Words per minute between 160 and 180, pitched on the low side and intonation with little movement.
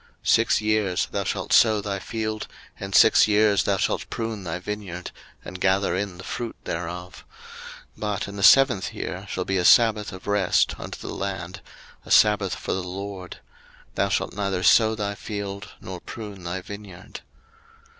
Yes: average, 175 wpm; low, 100 Hz; narrow, 2.3 semitones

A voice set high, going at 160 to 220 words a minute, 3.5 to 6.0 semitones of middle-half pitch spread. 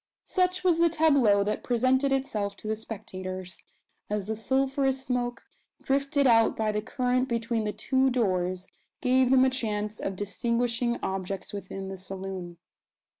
No: high, 230 Hz; average, 150 wpm; average, 4.7 semitones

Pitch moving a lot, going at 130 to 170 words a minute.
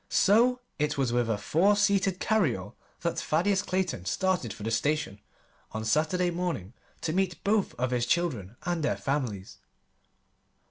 Yes: wide, 8.0 semitones; average, 150 wpm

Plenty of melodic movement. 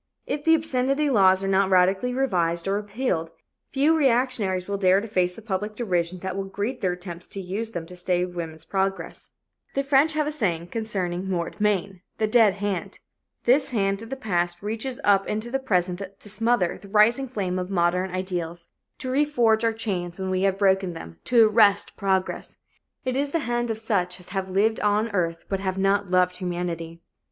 No: average, 4.0 semitones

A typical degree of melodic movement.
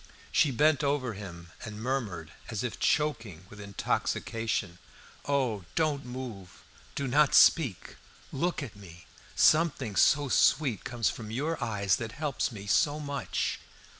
No: wide, 5.8 semitones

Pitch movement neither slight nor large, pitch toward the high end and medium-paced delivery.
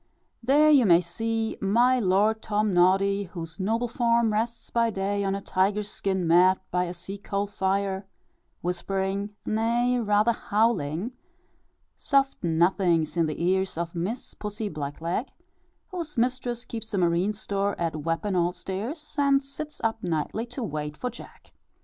Yes: average, 4.4 semitones; high, 200 Hz; average, 155 wpm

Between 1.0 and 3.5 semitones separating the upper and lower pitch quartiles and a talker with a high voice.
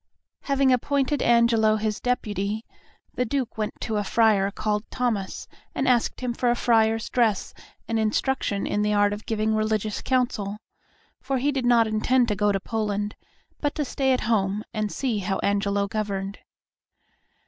Yes: average, 3.1 semitones; high, 220 Hz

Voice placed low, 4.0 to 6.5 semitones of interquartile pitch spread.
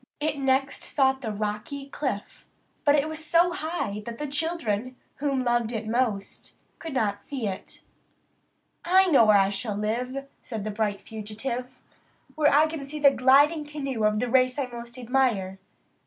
No: very high, 255 Hz; average, 4.9 semitones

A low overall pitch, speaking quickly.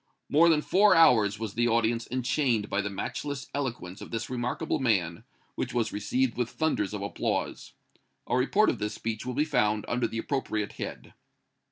No: low, 120 Hz; average, 180 wpm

